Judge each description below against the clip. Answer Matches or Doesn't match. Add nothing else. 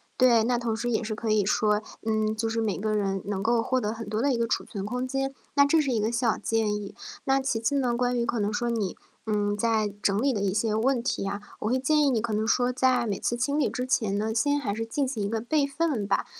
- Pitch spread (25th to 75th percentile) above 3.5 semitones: Doesn't match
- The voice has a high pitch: Matches